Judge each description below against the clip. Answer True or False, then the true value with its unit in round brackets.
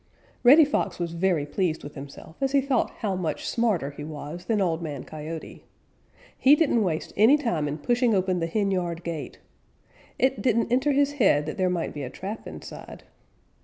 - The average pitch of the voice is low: False (185 Hz)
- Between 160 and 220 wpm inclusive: True (190 wpm)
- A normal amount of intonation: False (7.2 semitones)